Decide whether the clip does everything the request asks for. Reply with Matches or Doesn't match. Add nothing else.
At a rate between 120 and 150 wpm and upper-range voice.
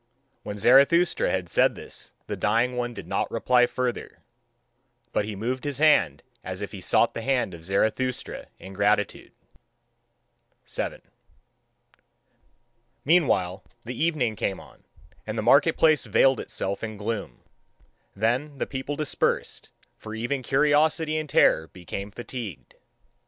Doesn't match